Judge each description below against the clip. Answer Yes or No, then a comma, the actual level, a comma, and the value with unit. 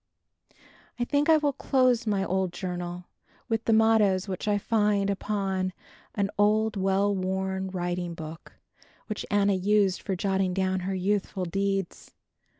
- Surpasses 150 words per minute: No, average, 145 wpm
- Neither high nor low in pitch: No, high, 195 Hz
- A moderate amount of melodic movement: No, narrow, 2.1 semitones